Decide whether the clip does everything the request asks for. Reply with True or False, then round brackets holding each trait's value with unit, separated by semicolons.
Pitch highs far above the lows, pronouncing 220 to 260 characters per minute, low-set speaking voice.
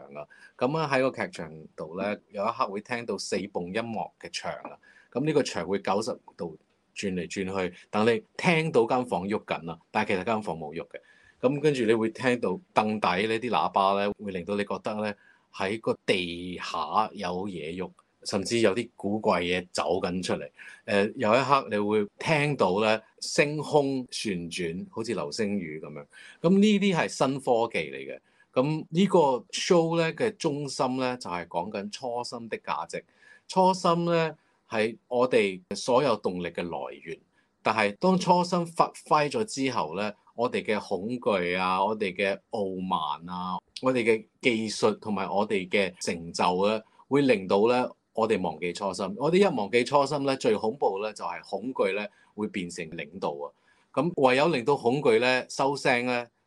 True (6.8 semitones; 250 characters per minute; 115 Hz)